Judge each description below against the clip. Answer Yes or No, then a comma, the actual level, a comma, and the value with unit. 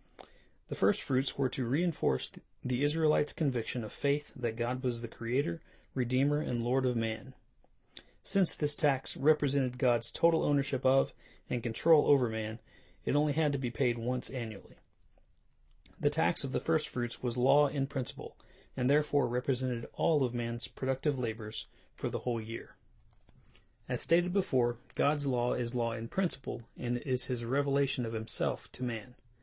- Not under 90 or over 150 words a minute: No, average, 165 wpm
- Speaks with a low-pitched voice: Yes, low, 125 Hz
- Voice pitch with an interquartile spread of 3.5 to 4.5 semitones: No, average, 2.9 semitones